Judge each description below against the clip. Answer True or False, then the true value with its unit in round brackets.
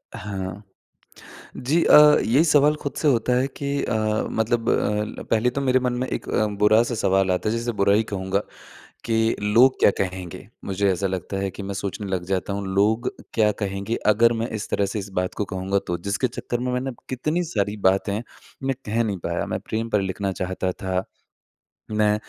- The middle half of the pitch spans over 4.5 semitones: False (3.6 semitones)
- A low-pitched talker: True (105 Hz)